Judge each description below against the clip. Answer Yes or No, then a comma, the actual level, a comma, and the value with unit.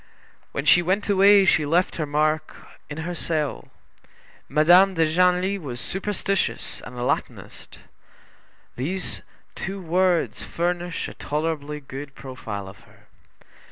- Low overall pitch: No, medium, 165 Hz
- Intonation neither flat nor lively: Yes, average, 4.0 semitones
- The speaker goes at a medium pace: No, slow, 125 wpm